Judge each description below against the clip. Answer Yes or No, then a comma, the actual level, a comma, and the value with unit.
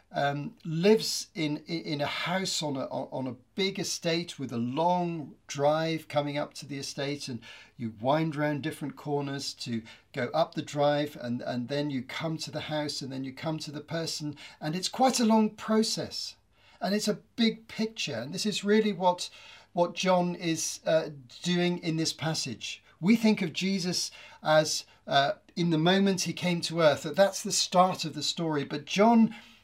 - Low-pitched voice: No, medium, 160 Hz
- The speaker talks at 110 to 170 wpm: No, average, 190 wpm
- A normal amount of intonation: Yes, average, 4.0 semitones